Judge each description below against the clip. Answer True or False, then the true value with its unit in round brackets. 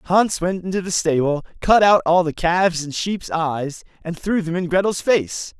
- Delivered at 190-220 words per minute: True (205 wpm)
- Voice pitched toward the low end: False (175 Hz)